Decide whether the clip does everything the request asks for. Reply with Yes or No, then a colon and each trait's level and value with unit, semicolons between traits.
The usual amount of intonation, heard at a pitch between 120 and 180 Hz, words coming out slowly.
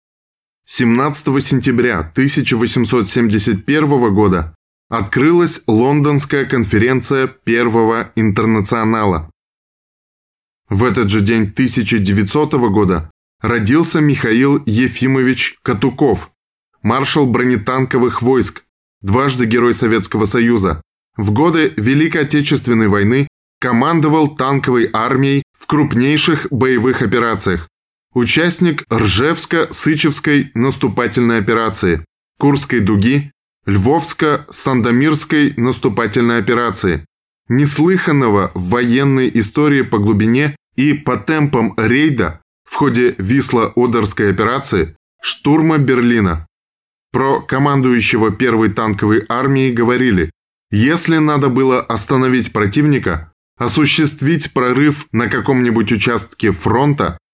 Yes: average, 4.2 semitones; low, 125 Hz; slow, 85 wpm